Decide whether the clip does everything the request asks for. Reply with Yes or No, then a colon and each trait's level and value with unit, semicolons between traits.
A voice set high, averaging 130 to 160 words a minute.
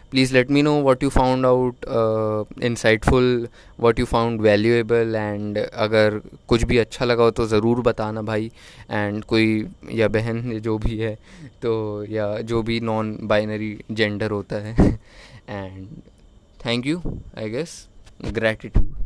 No: low, 110 Hz; average, 145 wpm